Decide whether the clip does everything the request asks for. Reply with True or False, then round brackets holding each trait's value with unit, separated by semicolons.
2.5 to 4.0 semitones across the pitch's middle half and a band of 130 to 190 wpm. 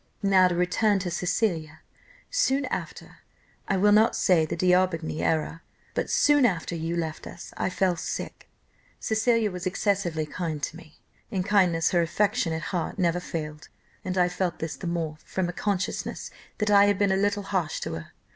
True (3.5 semitones; 175 wpm)